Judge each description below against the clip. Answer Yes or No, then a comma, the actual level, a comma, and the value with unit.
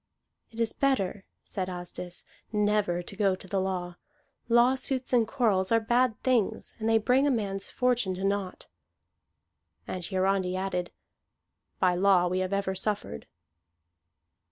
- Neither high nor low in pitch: No, high, 200 Hz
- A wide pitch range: No, average, 3.5 semitones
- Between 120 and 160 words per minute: Yes, average, 140 wpm